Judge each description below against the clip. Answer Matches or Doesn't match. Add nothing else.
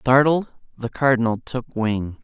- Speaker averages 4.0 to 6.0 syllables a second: Matches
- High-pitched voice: Doesn't match